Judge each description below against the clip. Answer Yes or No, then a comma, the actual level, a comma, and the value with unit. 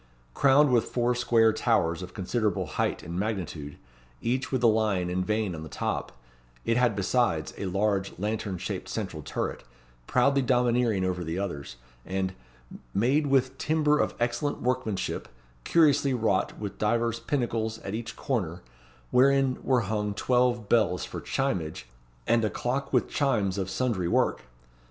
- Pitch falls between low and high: No, low, 110 Hz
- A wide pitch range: No, average, 4.7 semitones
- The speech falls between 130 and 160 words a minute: Yes, average, 150 wpm